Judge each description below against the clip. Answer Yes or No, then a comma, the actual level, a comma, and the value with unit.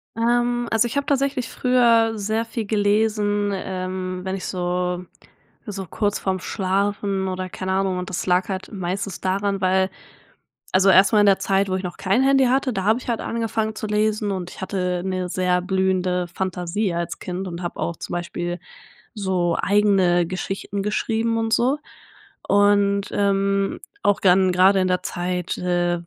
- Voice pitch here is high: Yes, high, 195 Hz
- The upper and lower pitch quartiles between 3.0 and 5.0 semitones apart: No, narrow, 2.5 semitones